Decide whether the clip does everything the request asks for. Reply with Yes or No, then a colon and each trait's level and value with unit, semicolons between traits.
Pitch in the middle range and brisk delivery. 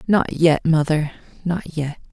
No: medium, 160 Hz; average, 140 wpm